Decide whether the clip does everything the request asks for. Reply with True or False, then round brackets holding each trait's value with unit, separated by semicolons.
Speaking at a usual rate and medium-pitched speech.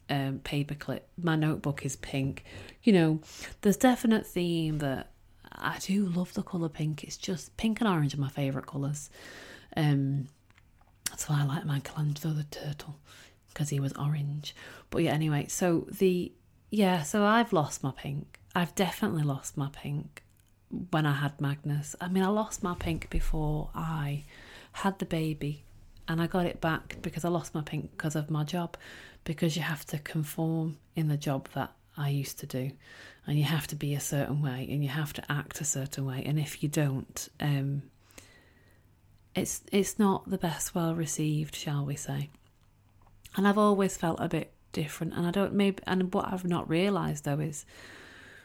True (180 wpm; 150 Hz)